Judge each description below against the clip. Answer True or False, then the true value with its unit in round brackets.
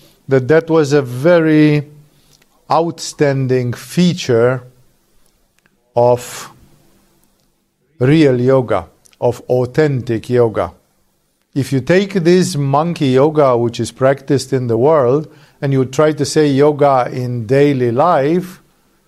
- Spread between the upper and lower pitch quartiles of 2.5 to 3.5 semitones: False (3.9 semitones)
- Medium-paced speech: False (105 wpm)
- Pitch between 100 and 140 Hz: True (135 Hz)